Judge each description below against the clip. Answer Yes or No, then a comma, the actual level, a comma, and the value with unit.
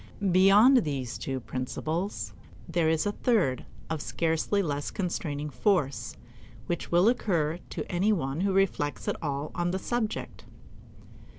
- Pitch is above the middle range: No, medium, 170 Hz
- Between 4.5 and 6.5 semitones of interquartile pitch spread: Yes, average, 5.0 semitones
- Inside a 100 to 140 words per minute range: Yes, slow, 135 wpm